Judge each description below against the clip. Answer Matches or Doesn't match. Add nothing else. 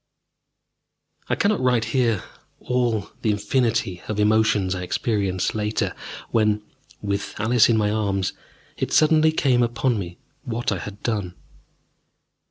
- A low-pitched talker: Matches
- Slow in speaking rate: Matches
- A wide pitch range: Doesn't match